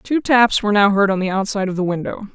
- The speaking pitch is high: Yes, high, 205 Hz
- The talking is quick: Yes, fast, 280 wpm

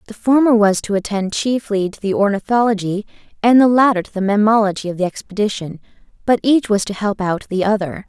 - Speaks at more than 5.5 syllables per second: Yes, 5.9 syllables/s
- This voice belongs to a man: No, female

